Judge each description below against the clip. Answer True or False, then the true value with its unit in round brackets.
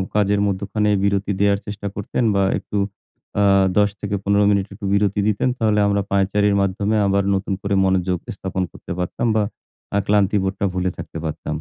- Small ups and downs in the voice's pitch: True (1.1 semitones)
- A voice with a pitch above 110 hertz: False (100 Hz)